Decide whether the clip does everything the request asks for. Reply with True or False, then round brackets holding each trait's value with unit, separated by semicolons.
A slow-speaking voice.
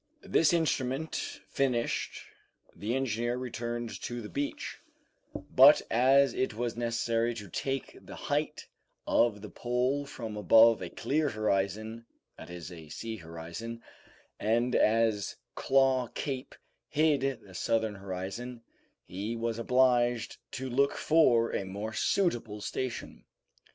True (125 wpm)